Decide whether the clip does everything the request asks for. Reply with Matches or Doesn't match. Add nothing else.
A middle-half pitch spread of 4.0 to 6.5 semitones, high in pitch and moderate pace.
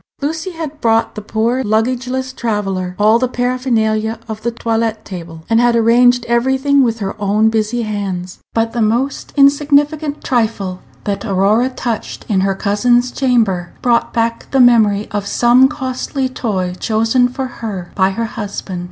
Doesn't match